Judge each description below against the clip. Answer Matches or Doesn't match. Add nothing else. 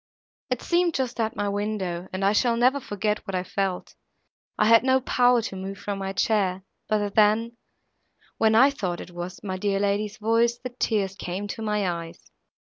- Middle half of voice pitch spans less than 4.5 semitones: Matches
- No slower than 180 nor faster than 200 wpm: Matches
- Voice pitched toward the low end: Doesn't match